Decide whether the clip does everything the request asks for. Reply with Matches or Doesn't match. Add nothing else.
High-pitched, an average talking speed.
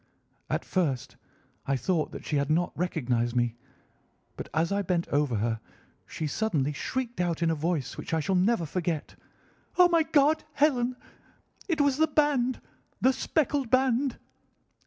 Doesn't match